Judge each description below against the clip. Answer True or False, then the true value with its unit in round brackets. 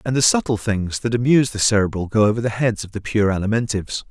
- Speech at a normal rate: False (235 wpm)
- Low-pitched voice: True (110 Hz)